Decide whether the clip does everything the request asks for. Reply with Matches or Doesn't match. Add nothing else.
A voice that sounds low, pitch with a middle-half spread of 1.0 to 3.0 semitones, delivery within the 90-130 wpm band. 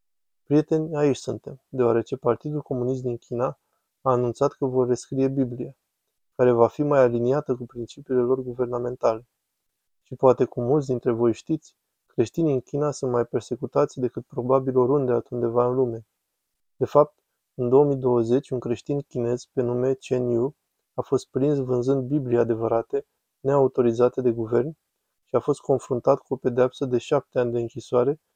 Doesn't match